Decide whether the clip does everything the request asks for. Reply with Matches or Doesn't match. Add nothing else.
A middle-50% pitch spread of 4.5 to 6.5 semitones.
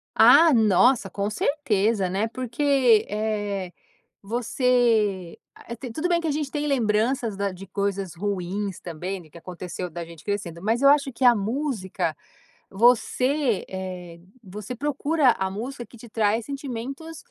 Matches